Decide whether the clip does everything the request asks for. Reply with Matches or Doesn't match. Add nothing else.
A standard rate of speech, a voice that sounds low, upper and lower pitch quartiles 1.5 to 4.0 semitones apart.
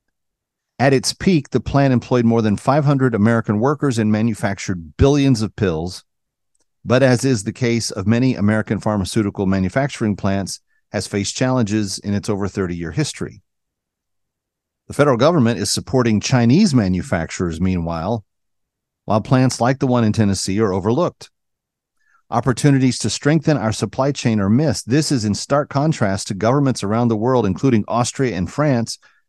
Doesn't match